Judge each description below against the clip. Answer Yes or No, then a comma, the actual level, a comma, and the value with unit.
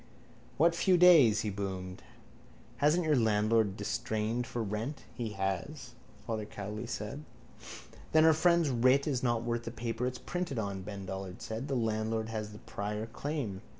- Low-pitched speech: Yes, low, 115 Hz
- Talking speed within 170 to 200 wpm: No, average, 160 wpm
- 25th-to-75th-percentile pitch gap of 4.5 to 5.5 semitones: Yes, average, 4.8 semitones